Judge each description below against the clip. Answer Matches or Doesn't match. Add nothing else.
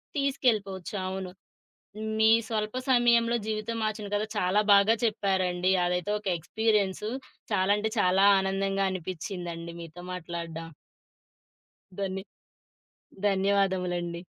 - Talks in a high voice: Matches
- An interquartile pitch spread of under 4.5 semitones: Matches